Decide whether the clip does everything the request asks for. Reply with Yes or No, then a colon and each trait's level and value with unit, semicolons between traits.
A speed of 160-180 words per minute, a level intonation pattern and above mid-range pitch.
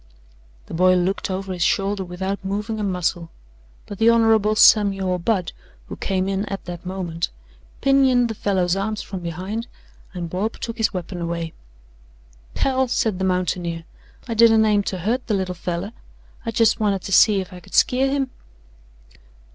No: average, 170 wpm; average, 3.4 semitones; high, 195 Hz